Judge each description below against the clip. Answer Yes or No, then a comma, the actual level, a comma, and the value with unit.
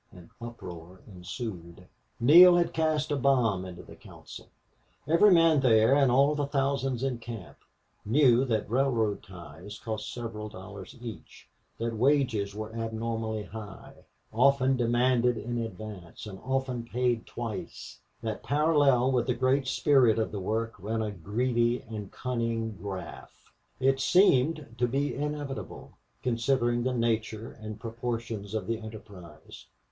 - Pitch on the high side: No, low, 115 Hz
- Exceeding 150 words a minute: No, average, 140 wpm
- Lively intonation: No, average, 3.6 semitones